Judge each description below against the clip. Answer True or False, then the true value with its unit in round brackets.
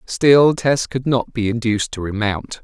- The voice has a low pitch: True (120 Hz)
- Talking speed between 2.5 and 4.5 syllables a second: True (4.4 syllables/s)